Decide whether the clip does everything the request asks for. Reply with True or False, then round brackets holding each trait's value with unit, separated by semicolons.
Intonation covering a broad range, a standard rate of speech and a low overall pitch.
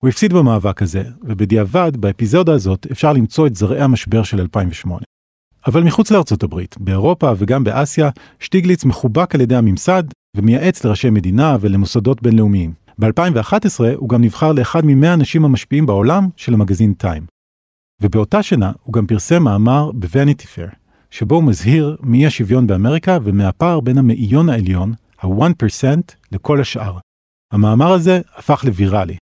True (6.6 semitones; 140 wpm; 120 Hz)